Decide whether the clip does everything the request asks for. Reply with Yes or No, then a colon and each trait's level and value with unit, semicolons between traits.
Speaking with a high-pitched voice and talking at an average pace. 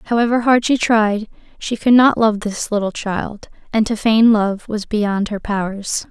Yes: high, 215 Hz; average, 185 wpm